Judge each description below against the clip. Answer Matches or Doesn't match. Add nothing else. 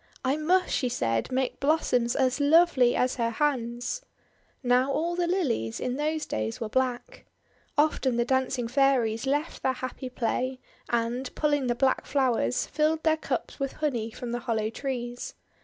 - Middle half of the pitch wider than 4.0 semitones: Doesn't match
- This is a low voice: Doesn't match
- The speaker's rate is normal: Matches